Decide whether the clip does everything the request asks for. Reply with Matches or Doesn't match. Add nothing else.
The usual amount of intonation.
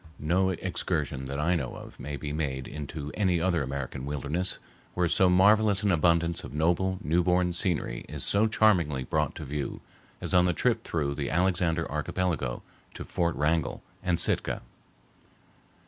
Matches